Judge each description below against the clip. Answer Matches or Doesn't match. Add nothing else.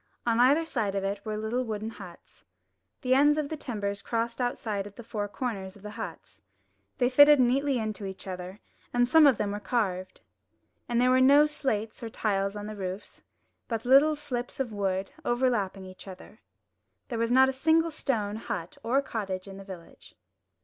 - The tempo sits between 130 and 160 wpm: Doesn't match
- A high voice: Matches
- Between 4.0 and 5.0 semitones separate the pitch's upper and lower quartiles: Matches